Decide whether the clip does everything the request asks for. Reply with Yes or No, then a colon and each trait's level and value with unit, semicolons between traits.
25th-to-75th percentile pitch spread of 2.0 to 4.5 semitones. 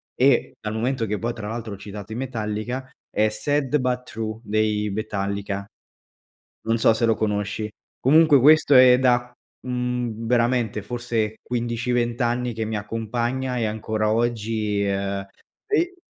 Yes: narrow, 2.4 semitones